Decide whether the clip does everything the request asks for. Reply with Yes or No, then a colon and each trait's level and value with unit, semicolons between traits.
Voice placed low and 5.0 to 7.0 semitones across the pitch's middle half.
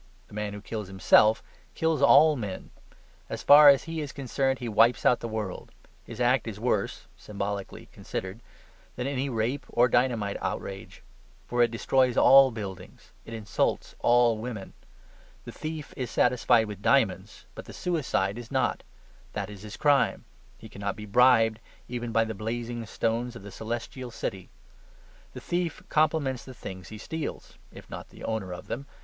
No: low, 115 Hz; average, 3.7 semitones